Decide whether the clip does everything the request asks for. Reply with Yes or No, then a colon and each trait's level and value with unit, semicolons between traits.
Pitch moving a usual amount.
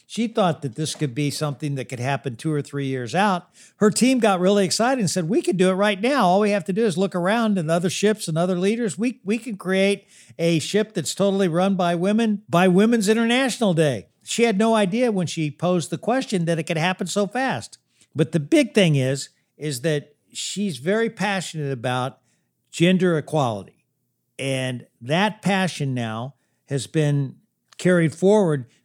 No: wide, 5.7 semitones